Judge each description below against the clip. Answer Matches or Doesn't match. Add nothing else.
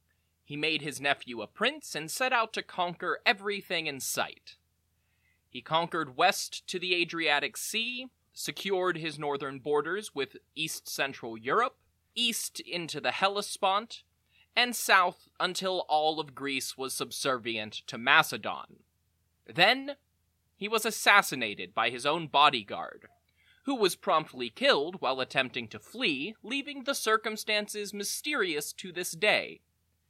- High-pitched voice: Doesn't match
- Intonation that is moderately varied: Doesn't match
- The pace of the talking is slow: Matches